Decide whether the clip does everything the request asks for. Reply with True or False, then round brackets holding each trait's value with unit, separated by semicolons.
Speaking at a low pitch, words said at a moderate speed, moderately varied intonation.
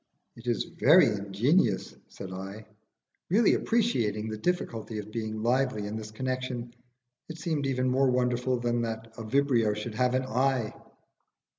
True (120 Hz; 150 wpm; 3.2 semitones)